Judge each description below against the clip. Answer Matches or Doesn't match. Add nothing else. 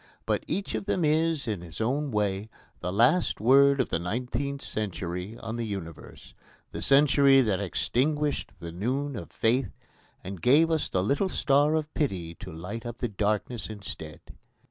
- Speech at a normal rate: Matches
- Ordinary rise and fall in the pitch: Doesn't match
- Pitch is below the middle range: Matches